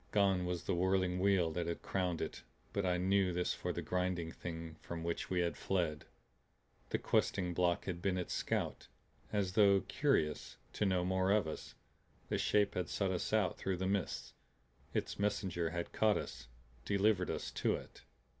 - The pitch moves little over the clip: Yes, narrow, 2.2 semitones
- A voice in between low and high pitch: No, very low, 90 Hz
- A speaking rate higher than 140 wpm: Yes, average, 180 wpm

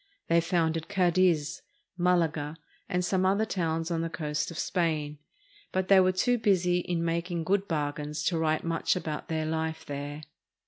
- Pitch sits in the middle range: Yes, medium, 165 Hz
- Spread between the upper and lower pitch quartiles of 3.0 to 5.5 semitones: No, narrow, 2.4 semitones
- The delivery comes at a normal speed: Yes, average, 165 wpm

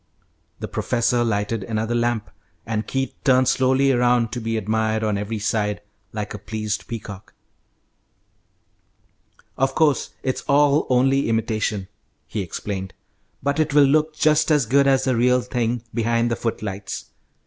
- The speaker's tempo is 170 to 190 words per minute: No, average, 145 wpm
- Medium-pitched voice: No, low, 115 Hz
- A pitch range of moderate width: Yes, average, 3.6 semitones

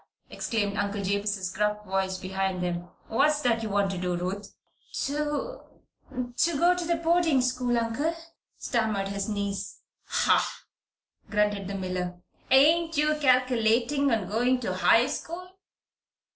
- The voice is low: No, high, 220 Hz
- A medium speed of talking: No, slow, 130 wpm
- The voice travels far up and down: Yes, wide, 6.4 semitones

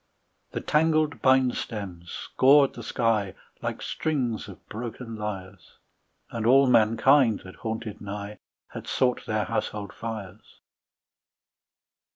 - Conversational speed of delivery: No, slow, 115 wpm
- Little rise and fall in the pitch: No, average, 4.0 semitones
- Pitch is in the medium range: No, low, 115 Hz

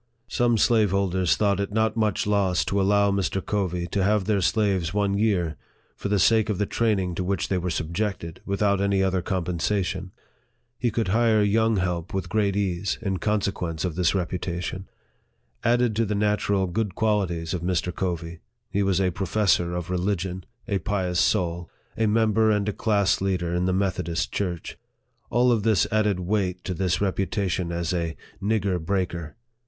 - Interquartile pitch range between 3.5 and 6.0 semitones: No, average, 2.7 semitones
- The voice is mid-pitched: No, very low, 95 Hz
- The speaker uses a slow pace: No, average, 180 wpm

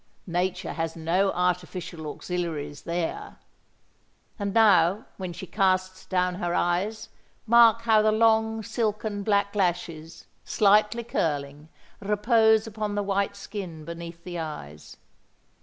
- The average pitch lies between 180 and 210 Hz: Yes, medium, 185 Hz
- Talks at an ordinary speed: No, slow, 120 wpm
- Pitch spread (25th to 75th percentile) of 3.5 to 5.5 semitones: Yes, average, 3.9 semitones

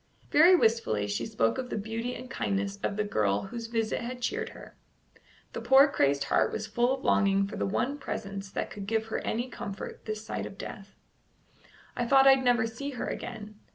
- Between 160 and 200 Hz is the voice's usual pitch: No, high, 220 Hz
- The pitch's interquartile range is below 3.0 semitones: No, average, 3.9 semitones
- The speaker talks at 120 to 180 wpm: No, average, 200 wpm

